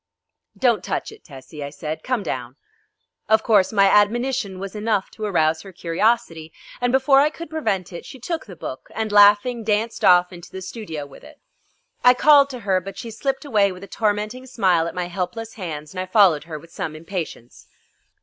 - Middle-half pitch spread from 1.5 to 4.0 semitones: No, average, 5.1 semitones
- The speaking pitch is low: No, high, 200 Hz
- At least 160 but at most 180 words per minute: No, average, 200 wpm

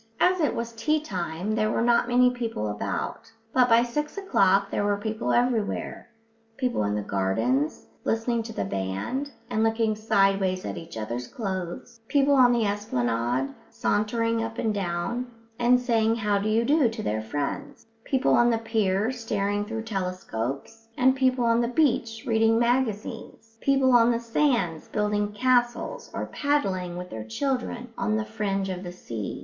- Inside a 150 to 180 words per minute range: Yes, average, 170 wpm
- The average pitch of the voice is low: No, high, 225 Hz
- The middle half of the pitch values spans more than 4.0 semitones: Yes, average, 4.5 semitones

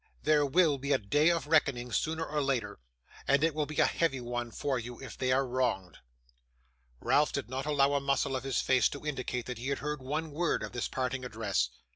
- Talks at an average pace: No, fast, 215 wpm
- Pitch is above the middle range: No, low, 135 Hz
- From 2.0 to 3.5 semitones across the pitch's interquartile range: Yes, average, 3.1 semitones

